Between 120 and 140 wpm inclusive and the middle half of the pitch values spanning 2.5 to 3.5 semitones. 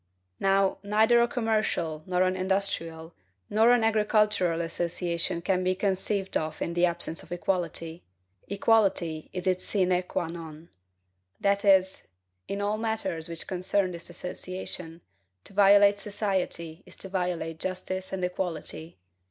Yes: slow, 135 wpm; average, 2.9 semitones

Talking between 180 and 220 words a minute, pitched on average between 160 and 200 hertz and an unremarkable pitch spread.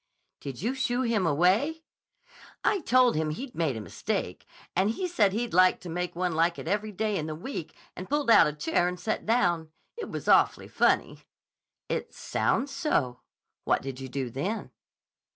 No: average, 185 wpm; medium, 185 Hz; wide, 7.2 semitones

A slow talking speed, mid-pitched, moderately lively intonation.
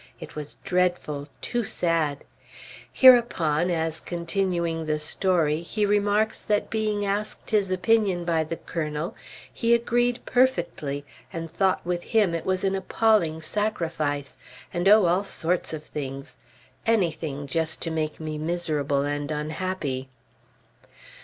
Yes: slow, 130 wpm; medium, 170 Hz; average, 4.6 semitones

